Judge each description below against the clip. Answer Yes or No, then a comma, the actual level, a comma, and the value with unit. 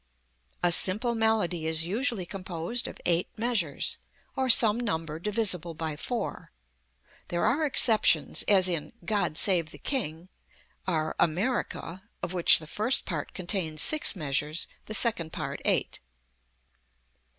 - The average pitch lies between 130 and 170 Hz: No, medium, 185 Hz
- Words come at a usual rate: No, slow, 130 wpm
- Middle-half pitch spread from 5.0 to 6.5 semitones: Yes, wide, 5.4 semitones